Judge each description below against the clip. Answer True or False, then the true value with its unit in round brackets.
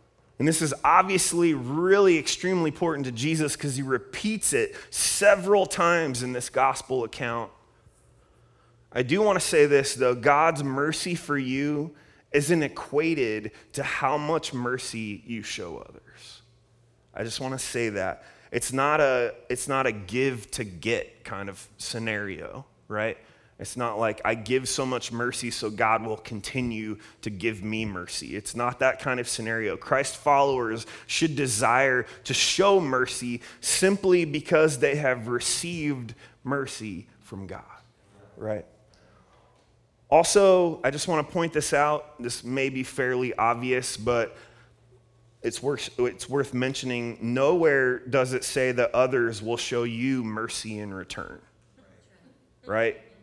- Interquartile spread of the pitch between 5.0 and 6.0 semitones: False (4.1 semitones)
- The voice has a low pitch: True (125 Hz)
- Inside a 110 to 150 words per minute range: True (145 wpm)